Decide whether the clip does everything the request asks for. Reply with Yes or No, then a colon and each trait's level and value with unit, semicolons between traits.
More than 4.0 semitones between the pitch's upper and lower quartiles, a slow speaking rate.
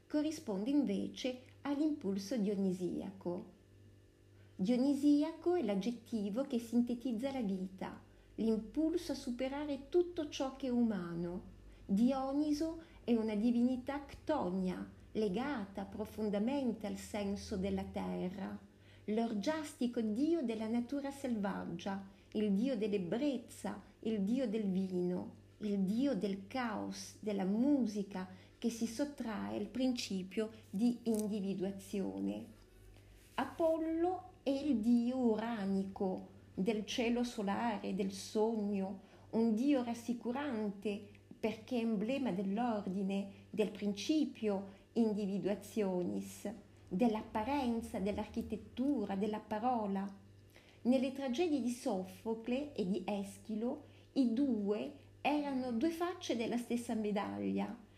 Yes: average, 4.7 semitones; slow, 95 wpm